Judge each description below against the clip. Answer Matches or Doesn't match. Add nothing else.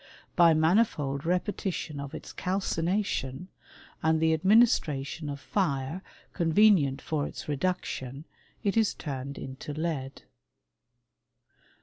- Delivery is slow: Matches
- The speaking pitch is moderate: Matches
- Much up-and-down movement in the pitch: Doesn't match